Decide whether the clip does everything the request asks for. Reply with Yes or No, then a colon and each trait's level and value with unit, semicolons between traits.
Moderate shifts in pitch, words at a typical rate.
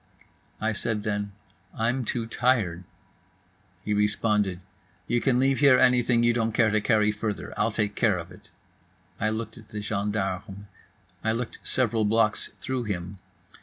No: narrow, 2.3 semitones; average, 155 wpm